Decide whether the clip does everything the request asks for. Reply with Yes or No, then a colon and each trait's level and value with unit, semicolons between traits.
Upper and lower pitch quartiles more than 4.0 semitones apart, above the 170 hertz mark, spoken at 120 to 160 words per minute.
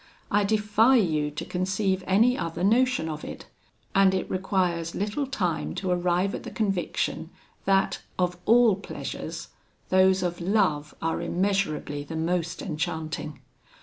No: average, 3.3 semitones; medium, 185 Hz; average, 140 wpm